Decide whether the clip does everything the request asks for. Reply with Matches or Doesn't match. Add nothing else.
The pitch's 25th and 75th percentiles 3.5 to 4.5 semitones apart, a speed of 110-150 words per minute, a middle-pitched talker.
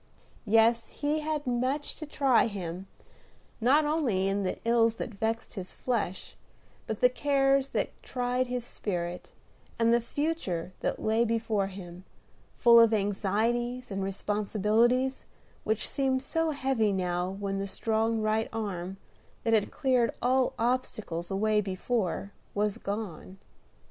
Doesn't match